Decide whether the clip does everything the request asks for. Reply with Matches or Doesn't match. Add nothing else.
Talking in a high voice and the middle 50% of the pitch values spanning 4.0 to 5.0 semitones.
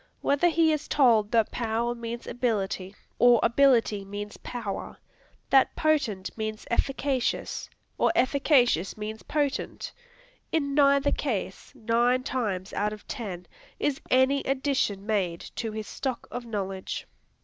Matches